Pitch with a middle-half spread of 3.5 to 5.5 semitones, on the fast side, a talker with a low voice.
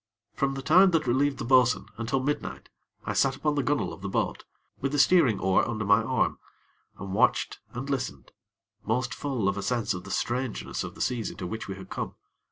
Yes: average, 4.3 semitones; fast, 215 wpm; low, 125 Hz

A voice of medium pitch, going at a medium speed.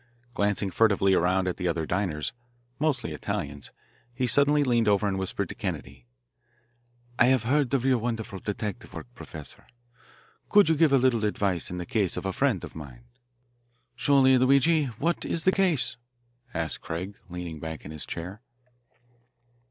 No: low, 105 Hz; average, 160 wpm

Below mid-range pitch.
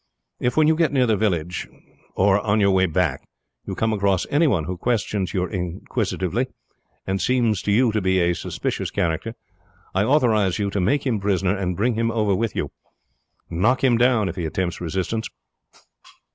Yes: low, 100 Hz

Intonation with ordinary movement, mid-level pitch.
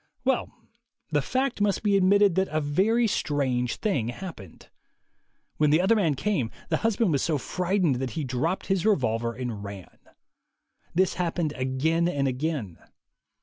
No: wide, 6.8 semitones; medium, 160 Hz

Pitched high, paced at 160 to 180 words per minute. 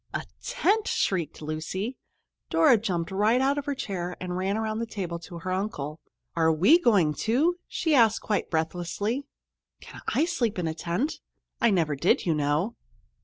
Yes: high, 195 Hz; average, 170 wpm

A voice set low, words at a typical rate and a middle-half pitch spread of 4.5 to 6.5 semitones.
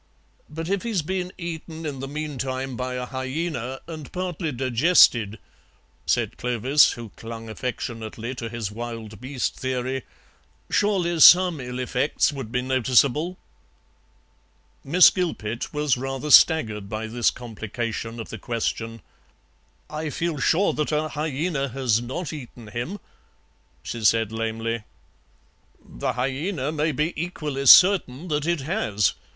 No: low, 130 Hz; slow, 130 wpm; average, 5.2 semitones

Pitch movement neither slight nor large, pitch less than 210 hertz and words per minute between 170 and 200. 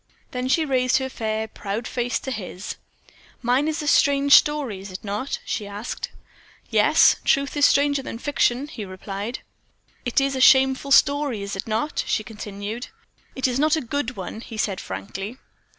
No: average, 4.9 semitones; high, 245 Hz; average, 180 wpm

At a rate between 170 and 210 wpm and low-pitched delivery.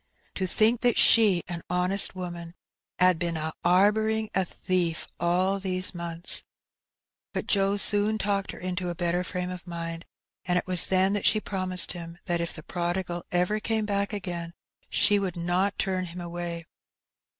No: average, 175 wpm; medium, 180 Hz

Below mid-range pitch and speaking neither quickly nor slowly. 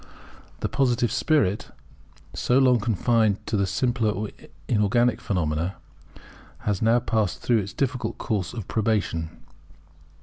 No: low, 110 Hz; slow, 115 wpm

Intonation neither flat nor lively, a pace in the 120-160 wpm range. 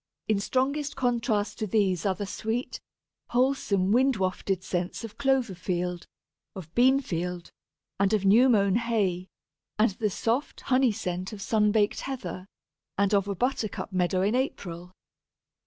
Yes: average, 4.7 semitones; average, 150 wpm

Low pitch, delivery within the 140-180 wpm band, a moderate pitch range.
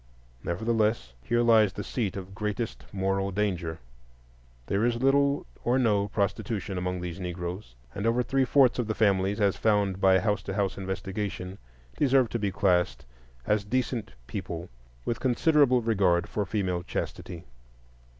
Yes: low, 100 Hz; average, 150 wpm; average, 3.7 semitones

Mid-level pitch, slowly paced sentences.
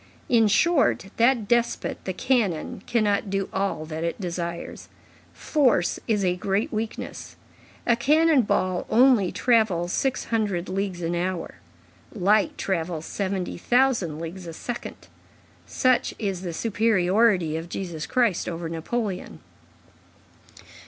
No: high, 195 Hz; slow, 125 wpm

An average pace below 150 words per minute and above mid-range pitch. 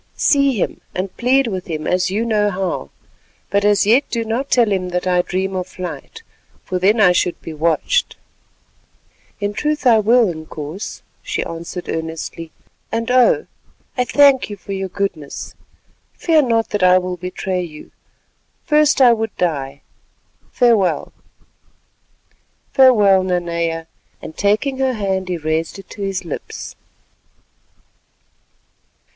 Yes: average, 140 wpm; high, 195 Hz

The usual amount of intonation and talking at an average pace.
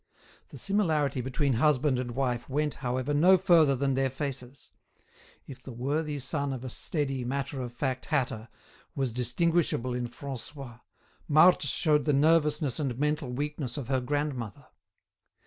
Yes: average, 3.0 semitones; average, 145 wpm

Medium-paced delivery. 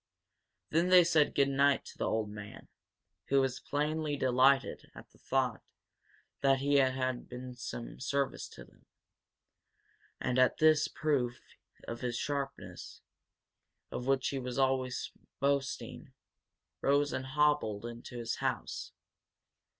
No: slow, 130 wpm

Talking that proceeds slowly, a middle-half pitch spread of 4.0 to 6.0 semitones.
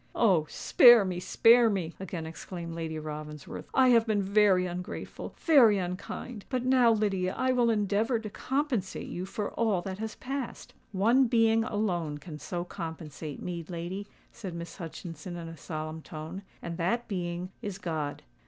No: average, 155 wpm; average, 5.0 semitones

